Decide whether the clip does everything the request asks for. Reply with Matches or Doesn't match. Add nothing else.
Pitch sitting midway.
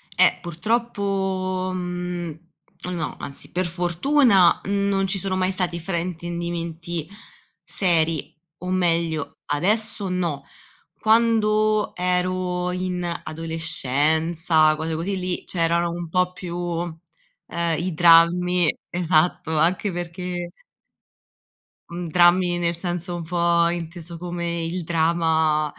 Matches